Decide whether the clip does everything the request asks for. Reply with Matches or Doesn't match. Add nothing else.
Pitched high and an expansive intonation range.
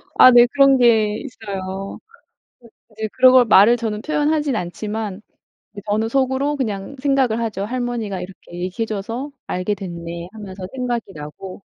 Doesn't match